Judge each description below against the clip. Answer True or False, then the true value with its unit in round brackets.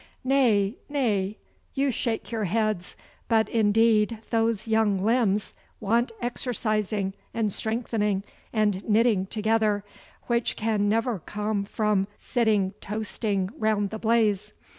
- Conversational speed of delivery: False (115 wpm)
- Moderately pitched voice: False (215 Hz)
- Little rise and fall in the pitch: True (1.9 semitones)